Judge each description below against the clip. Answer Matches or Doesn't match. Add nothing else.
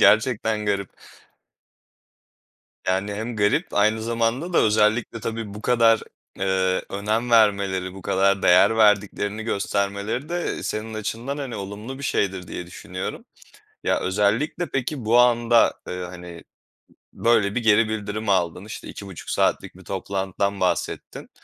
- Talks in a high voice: Doesn't match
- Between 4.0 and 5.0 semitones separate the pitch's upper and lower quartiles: Doesn't match